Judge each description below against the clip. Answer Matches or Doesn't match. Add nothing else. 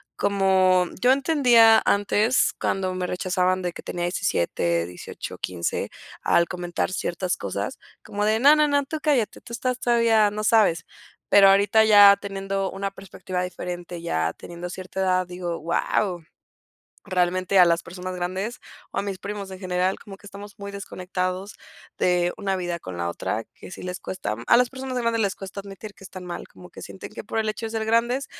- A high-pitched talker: Matches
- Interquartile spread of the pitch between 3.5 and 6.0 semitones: Doesn't match